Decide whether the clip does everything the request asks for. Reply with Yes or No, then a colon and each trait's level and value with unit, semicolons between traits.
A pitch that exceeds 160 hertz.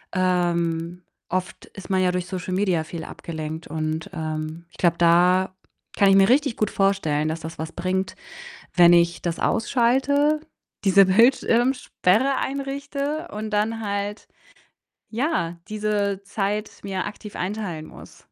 Yes: high, 190 Hz